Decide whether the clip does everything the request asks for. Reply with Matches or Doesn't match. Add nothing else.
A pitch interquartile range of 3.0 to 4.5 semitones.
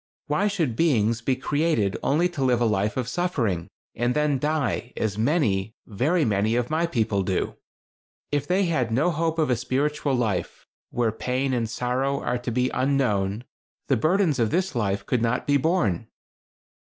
Doesn't match